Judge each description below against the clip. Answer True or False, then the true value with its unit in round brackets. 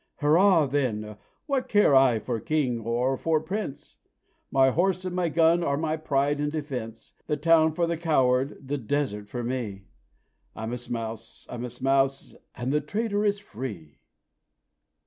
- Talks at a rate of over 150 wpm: True (160 wpm)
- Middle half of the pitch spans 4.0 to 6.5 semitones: True (4.9 semitones)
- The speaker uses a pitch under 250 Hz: True (140 Hz)